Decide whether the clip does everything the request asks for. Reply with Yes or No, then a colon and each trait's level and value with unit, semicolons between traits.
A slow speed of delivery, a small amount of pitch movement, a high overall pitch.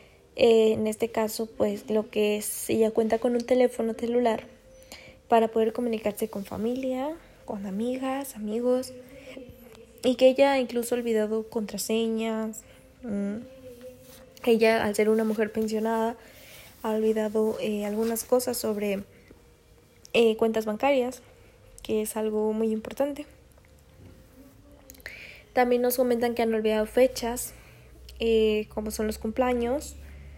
Yes: slow, 120 wpm; narrow, 2.2 semitones; high, 225 Hz